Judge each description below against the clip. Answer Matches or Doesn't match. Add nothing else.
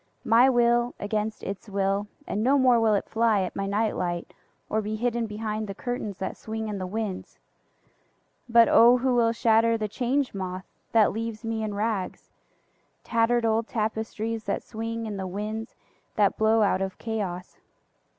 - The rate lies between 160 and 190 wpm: Matches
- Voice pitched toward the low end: Doesn't match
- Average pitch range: Doesn't match